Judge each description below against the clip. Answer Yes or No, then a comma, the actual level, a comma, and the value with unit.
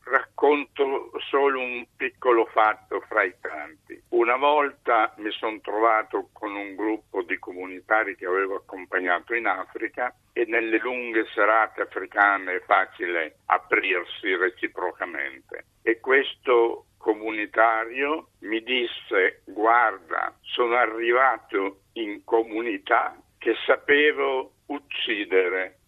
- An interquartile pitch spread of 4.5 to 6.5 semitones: Yes, average, 4.9 semitones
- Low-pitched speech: Yes, low, 125 Hz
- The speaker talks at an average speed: No, slow, 105 wpm